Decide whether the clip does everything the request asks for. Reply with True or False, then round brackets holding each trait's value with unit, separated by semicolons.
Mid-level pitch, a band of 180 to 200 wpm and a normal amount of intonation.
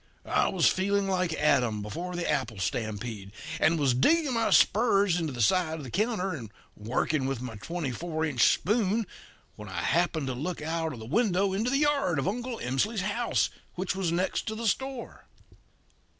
False (170 Hz; 185 wpm; 7.7 semitones)